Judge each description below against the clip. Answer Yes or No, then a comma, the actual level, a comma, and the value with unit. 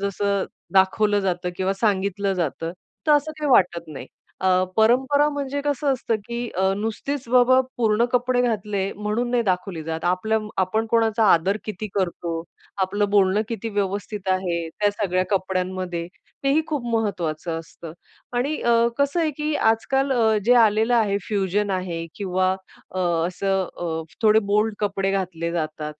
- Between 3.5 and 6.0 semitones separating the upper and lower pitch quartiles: Yes, average, 4.0 semitones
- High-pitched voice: Yes, high, 205 Hz